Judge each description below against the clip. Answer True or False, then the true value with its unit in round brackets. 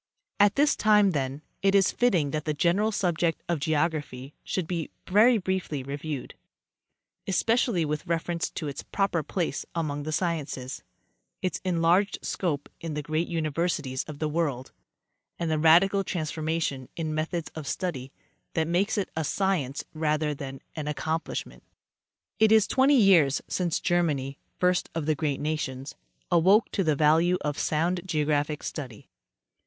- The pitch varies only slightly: False (3.5 semitones)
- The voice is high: False (160 Hz)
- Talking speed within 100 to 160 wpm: True (155 wpm)